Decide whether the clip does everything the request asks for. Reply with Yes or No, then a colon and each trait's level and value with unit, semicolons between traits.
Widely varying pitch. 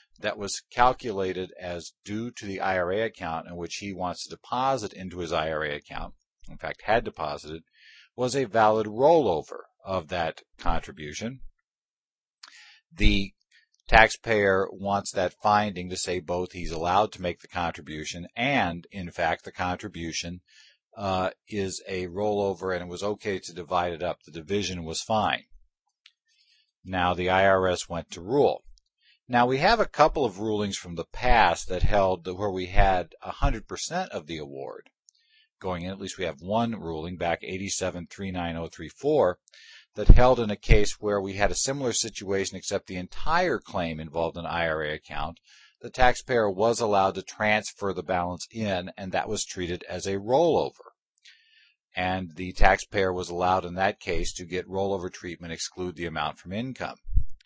No: average, 3.1 semitones